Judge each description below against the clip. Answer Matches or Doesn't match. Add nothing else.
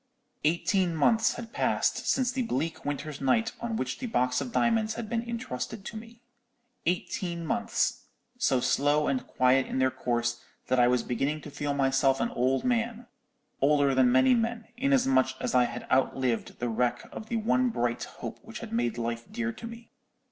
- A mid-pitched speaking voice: Matches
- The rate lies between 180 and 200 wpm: Matches